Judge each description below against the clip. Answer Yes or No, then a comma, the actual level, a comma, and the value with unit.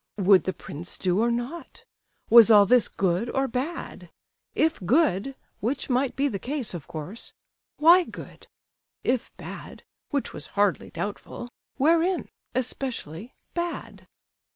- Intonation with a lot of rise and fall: Yes, wide, 6.1 semitones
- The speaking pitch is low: No, high, 240 Hz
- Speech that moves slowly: Yes, slow, 130 wpm